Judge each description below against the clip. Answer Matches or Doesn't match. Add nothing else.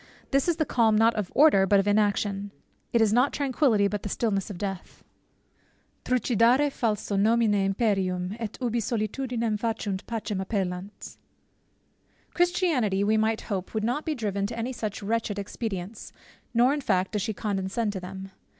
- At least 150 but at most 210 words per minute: Matches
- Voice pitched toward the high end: Matches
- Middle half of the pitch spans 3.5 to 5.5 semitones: Doesn't match